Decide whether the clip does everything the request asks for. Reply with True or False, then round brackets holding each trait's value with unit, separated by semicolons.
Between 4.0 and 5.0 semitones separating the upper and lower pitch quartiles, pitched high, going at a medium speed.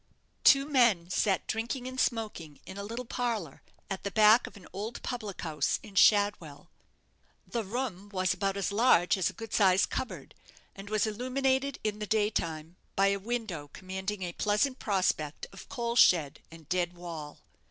True (4.4 semitones; 205 Hz; 175 wpm)